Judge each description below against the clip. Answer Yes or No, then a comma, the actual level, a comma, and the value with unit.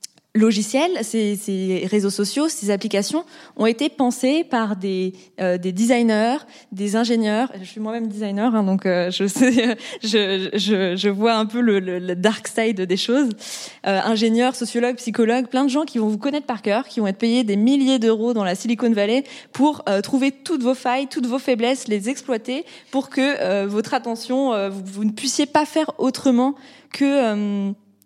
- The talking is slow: No, average, 190 wpm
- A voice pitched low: No, high, 230 Hz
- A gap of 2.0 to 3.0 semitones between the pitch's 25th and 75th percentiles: No, average, 4.3 semitones